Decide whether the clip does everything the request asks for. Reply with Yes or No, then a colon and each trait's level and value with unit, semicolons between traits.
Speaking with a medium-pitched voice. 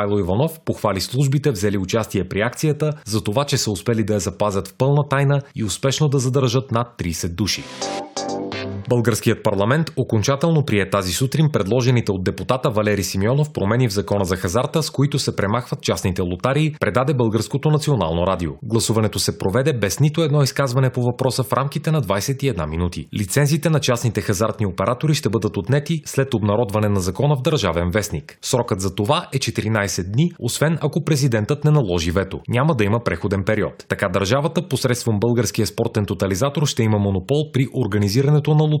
No: low, 115 Hz